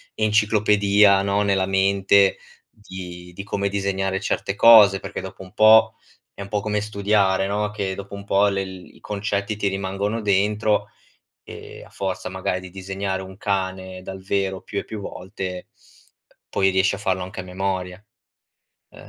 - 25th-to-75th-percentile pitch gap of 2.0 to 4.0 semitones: No, narrow, 1.4 semitones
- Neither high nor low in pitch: No, low, 100 Hz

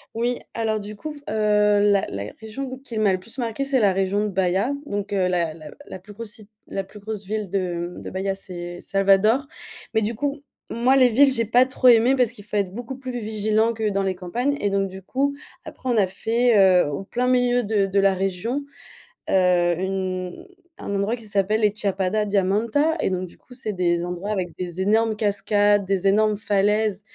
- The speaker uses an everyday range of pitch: Yes, average, 3.3 semitones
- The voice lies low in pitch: No, high, 205 Hz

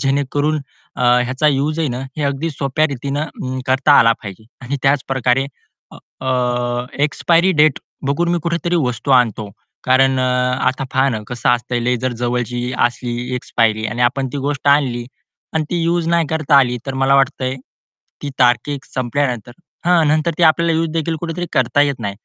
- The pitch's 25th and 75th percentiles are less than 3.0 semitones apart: No, average, 3.7 semitones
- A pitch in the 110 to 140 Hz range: Yes, low, 135 Hz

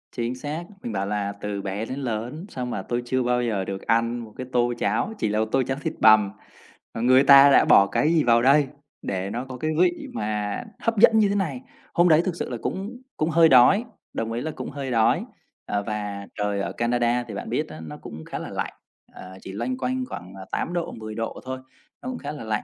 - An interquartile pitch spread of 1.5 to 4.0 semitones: No, average, 5.1 semitones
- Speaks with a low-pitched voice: Yes, low, 120 Hz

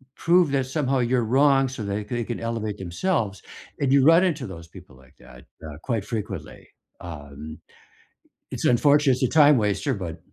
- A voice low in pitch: Yes, low, 120 Hz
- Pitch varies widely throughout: Yes, wide, 6.3 semitones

